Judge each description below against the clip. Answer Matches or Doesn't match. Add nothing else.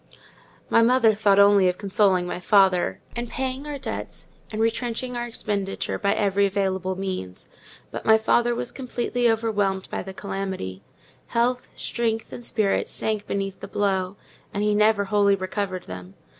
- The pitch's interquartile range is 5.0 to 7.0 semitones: Doesn't match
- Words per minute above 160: Doesn't match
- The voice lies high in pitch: Matches